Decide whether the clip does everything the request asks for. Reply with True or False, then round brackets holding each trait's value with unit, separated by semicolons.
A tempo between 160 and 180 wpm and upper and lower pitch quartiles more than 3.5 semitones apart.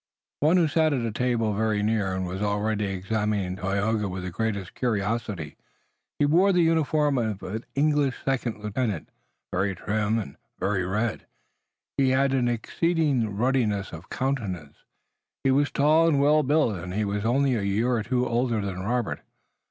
True (165 wpm; 5.1 semitones)